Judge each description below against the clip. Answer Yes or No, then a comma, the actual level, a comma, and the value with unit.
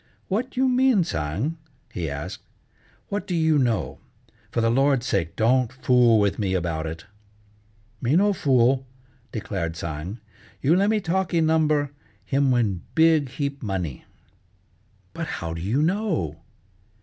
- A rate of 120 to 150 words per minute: Yes, average, 140 wpm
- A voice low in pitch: Yes, low, 130 Hz